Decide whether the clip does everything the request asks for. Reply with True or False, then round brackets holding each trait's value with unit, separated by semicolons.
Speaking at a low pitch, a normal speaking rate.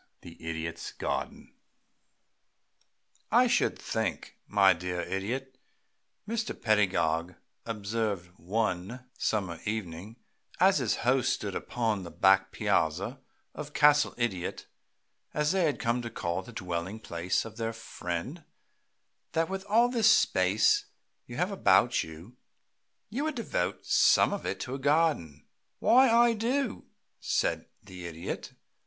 False (110 Hz; 130 wpm)